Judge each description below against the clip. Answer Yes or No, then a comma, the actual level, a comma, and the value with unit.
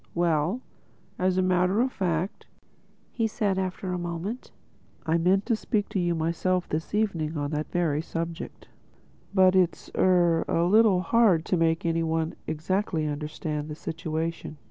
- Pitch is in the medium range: Yes, medium, 175 Hz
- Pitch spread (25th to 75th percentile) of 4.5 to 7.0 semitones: No, average, 2.7 semitones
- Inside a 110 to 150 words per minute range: Yes, average, 145 wpm